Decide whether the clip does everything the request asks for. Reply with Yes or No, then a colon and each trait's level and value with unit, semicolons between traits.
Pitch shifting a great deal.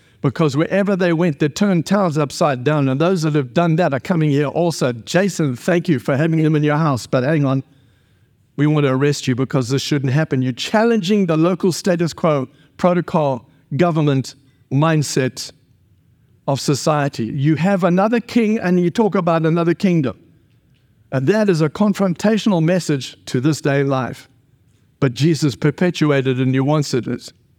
No: average, 4.6 semitones